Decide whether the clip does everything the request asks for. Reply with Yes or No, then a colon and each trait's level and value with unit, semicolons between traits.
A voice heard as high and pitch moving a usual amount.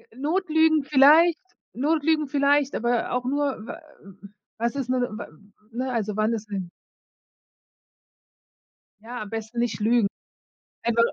Yes: very high, 250 Hz; average, 4.4 semitones